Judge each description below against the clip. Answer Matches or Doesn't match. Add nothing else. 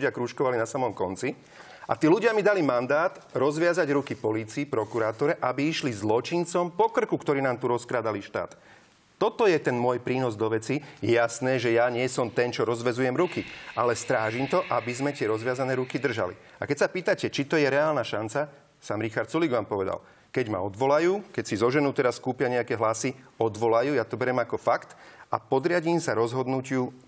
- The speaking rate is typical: Doesn't match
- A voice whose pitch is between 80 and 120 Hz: Doesn't match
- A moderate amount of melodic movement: Matches